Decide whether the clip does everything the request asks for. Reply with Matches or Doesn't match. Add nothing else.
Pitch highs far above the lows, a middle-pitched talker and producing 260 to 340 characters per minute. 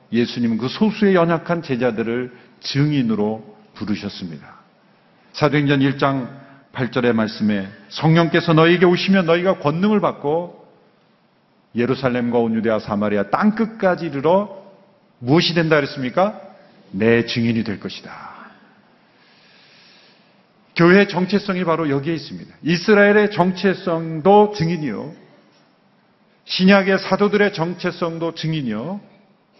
Matches